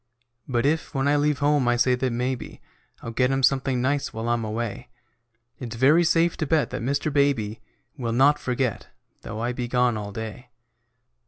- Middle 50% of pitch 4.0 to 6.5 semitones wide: No, average, 3.2 semitones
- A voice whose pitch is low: Yes, low, 125 Hz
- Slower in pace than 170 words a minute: No, average, 185 wpm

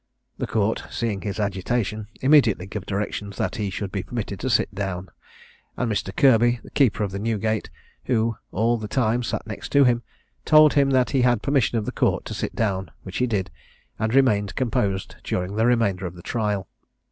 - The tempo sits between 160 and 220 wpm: Yes, average, 190 wpm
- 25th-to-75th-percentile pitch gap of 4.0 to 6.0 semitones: No, average, 3.6 semitones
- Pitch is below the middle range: Yes, low, 110 Hz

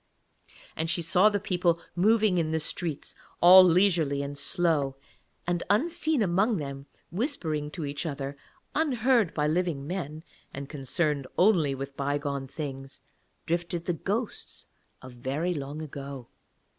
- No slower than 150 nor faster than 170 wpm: No, slow, 135 wpm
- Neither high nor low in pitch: Yes, medium, 160 Hz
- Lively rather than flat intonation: No, average, 4.7 semitones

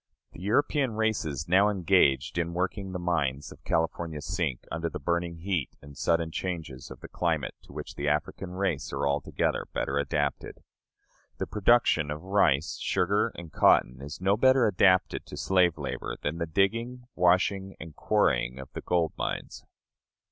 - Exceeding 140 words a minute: Yes, average, 160 wpm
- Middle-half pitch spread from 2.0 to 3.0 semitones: No, average, 4.5 semitones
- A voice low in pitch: Yes, very low, 85 Hz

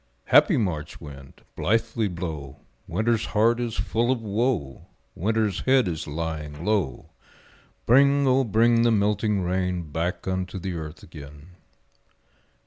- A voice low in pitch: Yes, very low, 95 Hz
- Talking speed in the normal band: No, slow, 130 wpm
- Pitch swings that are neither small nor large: No, wide, 5.9 semitones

